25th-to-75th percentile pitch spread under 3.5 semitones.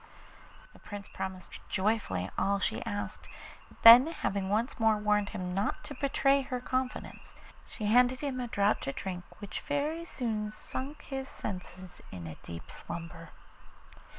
No: average, 5.3 semitones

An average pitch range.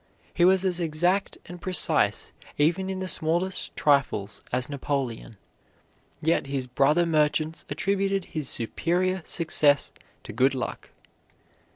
Yes: average, 4.8 semitones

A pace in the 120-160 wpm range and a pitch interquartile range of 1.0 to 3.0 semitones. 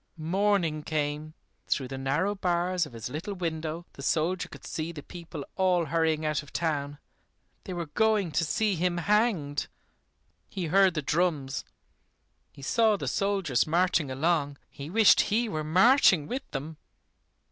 No: average, 155 wpm; average, 4.0 semitones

